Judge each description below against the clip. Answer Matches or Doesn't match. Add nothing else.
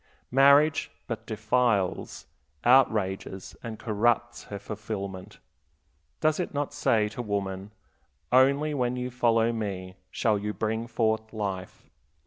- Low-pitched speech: Matches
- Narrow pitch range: Doesn't match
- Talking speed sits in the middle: Doesn't match